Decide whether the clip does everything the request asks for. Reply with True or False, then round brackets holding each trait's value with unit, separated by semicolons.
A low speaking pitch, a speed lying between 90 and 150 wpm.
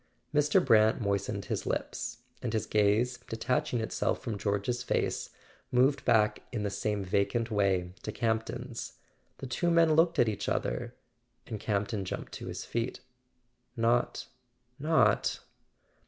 True (115 Hz; 140 wpm)